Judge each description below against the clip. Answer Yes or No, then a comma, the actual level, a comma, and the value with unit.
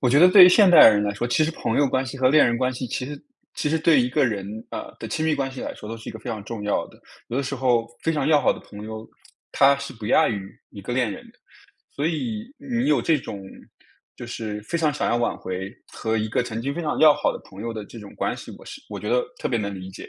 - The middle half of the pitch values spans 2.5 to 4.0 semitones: No, average, 5.3 semitones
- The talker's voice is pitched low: Yes, low, 125 Hz